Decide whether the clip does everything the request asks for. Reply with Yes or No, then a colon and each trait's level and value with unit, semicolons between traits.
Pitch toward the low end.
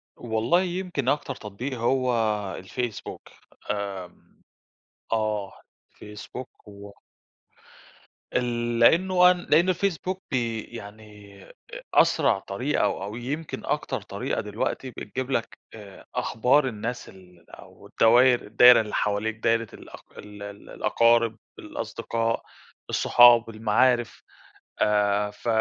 Yes: low, 115 Hz